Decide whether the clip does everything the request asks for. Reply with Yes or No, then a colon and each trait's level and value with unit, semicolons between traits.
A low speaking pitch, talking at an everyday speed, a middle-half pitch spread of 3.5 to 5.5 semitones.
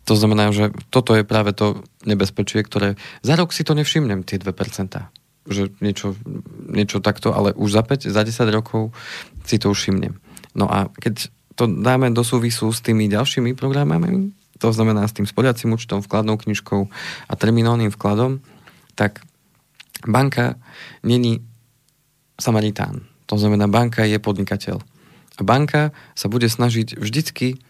Yes: low, 115 Hz; average, 145 wpm; average, 3.9 semitones